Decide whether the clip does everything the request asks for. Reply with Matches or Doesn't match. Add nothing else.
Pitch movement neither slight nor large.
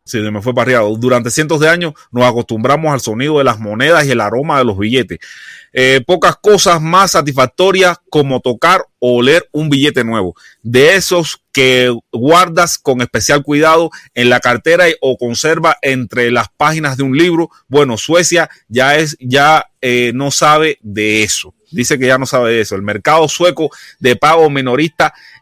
Matches